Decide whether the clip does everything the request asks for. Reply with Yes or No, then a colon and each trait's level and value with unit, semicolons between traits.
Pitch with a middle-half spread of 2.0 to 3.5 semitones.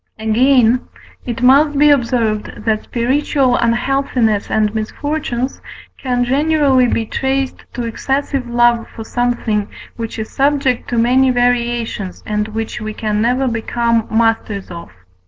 Yes: average, 3.0 semitones